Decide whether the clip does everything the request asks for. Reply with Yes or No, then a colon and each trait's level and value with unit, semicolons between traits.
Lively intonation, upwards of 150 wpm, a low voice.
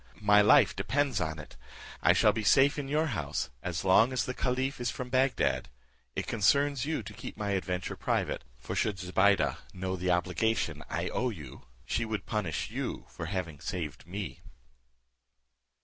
Yes: wide, 6.1 semitones; average, 170 wpm; low, 105 Hz